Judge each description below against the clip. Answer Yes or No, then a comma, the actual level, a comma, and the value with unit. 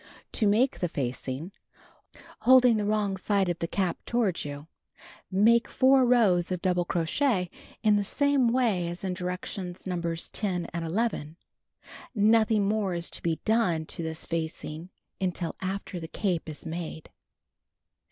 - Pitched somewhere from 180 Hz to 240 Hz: Yes, medium, 185 Hz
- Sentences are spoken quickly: No, average, 150 wpm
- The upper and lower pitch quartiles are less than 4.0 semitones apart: No, average, 4.3 semitones